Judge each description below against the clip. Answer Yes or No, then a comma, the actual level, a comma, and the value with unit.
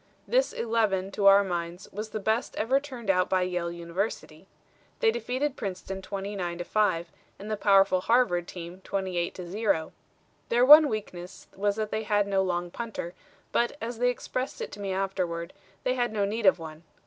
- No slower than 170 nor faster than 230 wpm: Yes, average, 185 wpm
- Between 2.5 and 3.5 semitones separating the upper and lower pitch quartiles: No, average, 3.9 semitones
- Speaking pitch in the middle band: No, high, 200 Hz